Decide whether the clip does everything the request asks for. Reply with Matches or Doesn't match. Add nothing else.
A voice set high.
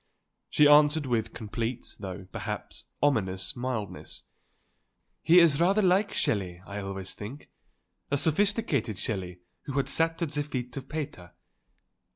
Doesn't match